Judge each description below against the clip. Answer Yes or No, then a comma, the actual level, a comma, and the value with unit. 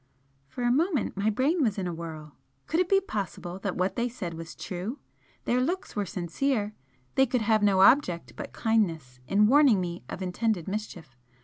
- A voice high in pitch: Yes, high, 205 Hz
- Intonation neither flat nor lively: No, wide, 6.0 semitones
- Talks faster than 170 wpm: Yes, average, 190 wpm